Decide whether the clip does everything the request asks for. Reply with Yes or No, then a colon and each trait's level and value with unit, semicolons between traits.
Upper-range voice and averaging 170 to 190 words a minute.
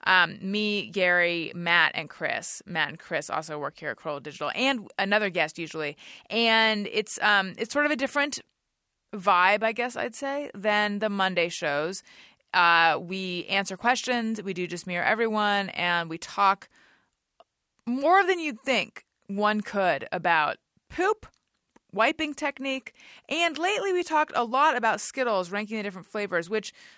No: high, 210 Hz; average, 160 wpm